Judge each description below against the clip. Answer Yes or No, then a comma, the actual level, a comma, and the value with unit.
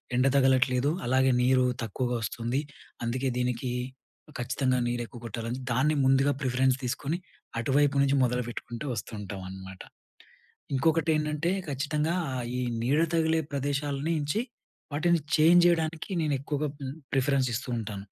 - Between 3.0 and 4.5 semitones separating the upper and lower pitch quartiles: Yes, average, 3.3 semitones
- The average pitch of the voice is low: Yes, low, 130 Hz